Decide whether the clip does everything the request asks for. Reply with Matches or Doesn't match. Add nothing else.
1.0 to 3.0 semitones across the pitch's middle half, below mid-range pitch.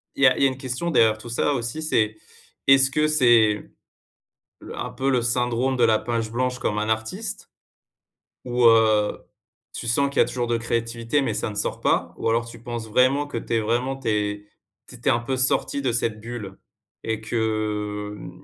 Matches